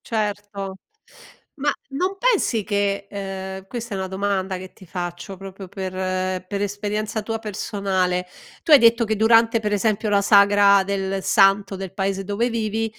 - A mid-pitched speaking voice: No, high, 200 Hz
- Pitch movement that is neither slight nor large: No, narrow, 2.2 semitones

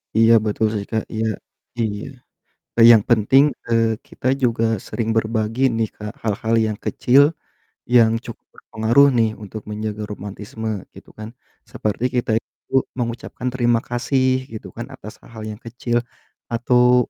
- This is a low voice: Yes, low, 115 Hz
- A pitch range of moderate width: No, narrow, 1.9 semitones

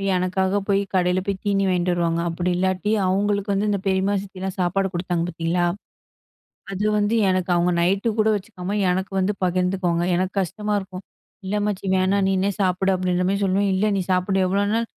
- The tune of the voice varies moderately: No, narrow, 1.7 semitones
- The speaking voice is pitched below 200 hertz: Yes, high, 190 Hz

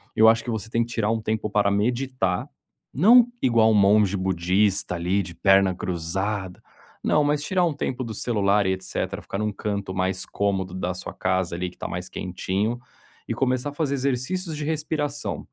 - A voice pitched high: No, low, 105 Hz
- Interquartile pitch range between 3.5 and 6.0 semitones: Yes, average, 5.3 semitones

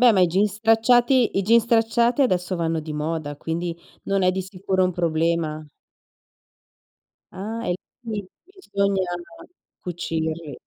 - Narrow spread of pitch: No, average, 5.2 semitones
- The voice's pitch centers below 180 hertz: No, medium, 185 Hz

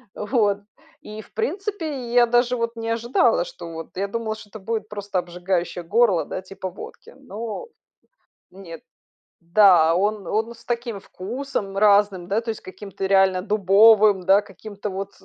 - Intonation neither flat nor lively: Yes, average, 3.2 semitones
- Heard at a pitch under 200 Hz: No, high, 210 Hz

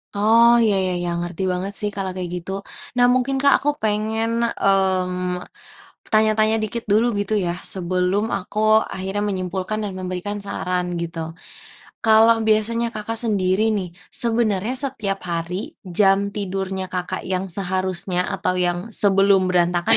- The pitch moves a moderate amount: Yes, average, 3.0 semitones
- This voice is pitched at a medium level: No, high, 195 Hz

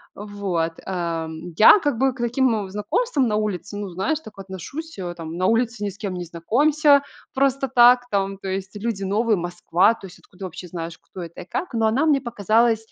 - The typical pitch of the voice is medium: No, high, 205 Hz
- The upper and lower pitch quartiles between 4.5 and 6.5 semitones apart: Yes, average, 5.0 semitones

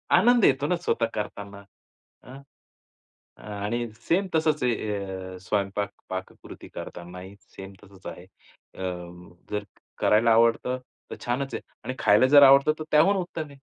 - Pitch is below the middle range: Yes, low, 115 Hz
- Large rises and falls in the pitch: Yes, wide, 5.7 semitones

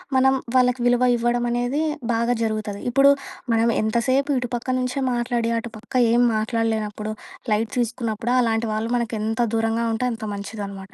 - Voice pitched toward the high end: Yes, high, 230 Hz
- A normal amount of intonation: No, narrow, 1.9 semitones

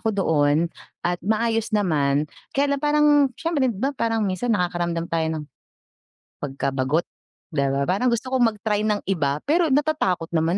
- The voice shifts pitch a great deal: Yes, wide, 7.1 semitones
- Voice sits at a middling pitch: No, high, 195 Hz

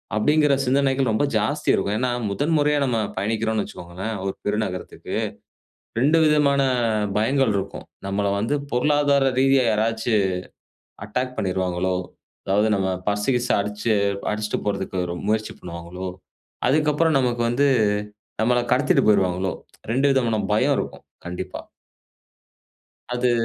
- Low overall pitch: Yes, low, 115 Hz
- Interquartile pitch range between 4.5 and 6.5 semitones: Yes, average, 5.3 semitones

